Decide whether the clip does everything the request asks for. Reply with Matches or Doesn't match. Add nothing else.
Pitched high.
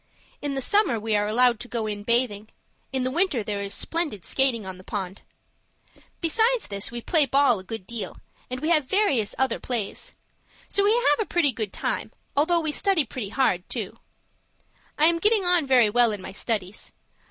Matches